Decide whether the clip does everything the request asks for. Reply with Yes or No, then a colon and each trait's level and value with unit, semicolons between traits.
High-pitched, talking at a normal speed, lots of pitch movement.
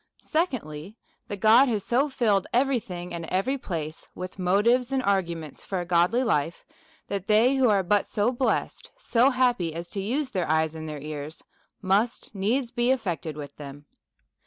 Yes: high, 200 Hz; average, 175 wpm; wide, 6.4 semitones